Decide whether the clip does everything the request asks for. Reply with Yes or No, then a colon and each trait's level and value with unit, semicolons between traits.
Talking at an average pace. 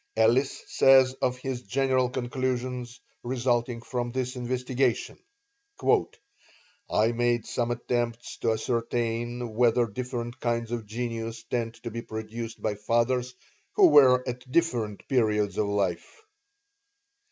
No: slow, 120 wpm